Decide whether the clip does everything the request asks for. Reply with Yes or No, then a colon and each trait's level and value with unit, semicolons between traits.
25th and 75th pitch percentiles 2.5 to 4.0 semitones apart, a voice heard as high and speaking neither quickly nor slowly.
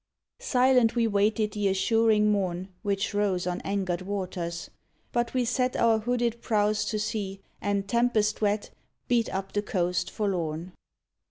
Yes: average, 3.0 semitones; high, 205 Hz; average, 145 wpm